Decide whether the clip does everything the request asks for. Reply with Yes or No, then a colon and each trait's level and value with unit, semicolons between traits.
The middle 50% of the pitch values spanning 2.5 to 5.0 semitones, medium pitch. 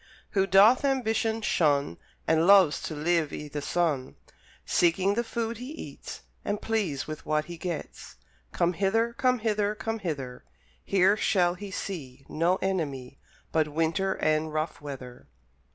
No: wide, 5.4 semitones; medium, 175 Hz